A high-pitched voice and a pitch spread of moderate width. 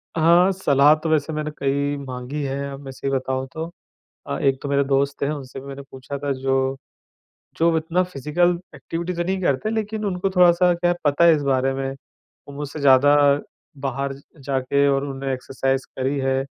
No: medium, 140 Hz; average, 3.5 semitones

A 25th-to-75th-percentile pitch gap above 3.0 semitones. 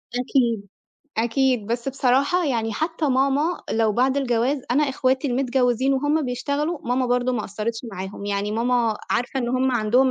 No: average, 2.7 semitones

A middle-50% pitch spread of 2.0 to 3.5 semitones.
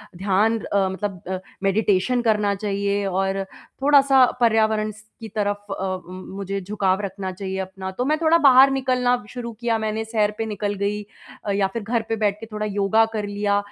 Yes: narrow, 2.4 semitones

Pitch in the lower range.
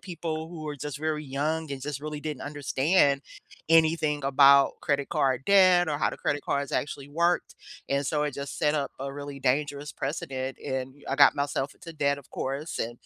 No: medium, 145 Hz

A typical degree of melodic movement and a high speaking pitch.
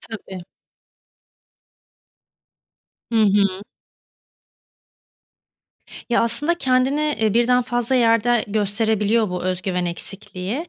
Yes: average, 3.7 semitones; high, 220 Hz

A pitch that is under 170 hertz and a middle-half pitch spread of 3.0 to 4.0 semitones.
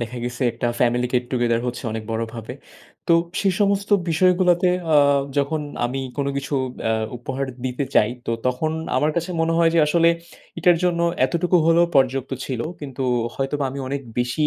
No: medium, 140 Hz; average, 5.2 semitones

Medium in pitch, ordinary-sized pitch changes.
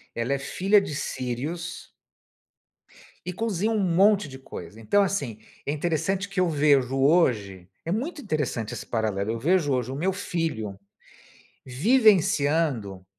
No: medium, 150 Hz; wide, 7.2 semitones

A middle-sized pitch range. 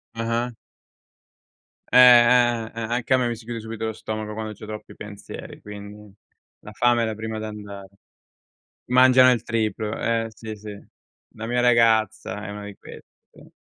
No: narrow, 2.0 semitones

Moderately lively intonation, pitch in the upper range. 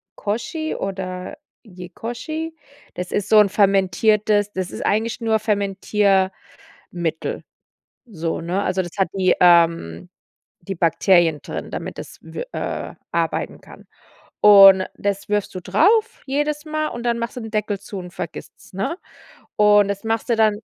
Yes: average, 3.2 semitones; high, 205 Hz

